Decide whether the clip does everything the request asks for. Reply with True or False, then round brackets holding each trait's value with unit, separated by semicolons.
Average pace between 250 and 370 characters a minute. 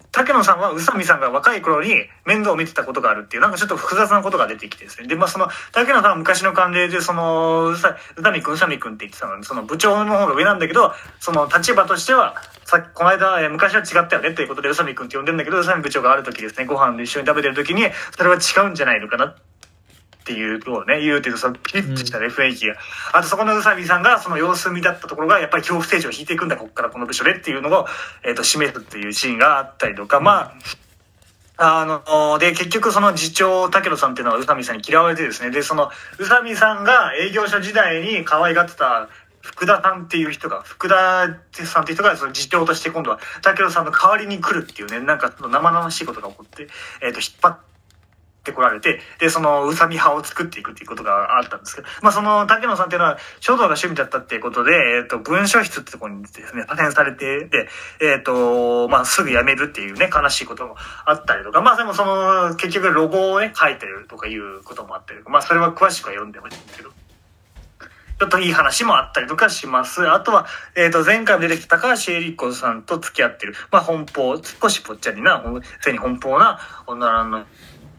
False (465 characters per minute)